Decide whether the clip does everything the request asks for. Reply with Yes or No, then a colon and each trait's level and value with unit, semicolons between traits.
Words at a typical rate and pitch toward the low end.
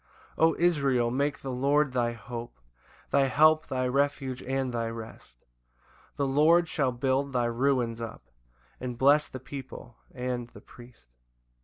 Yes: average, 155 wpm; low, 130 Hz